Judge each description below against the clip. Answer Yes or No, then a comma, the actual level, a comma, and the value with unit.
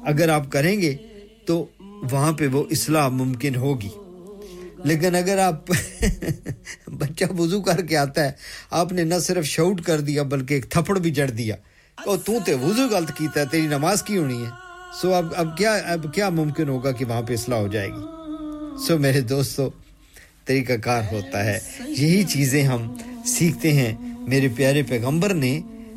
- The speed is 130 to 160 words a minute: No, average, 175 wpm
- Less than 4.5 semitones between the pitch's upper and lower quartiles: No, average, 5.2 semitones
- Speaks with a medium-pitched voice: Yes, medium, 155 Hz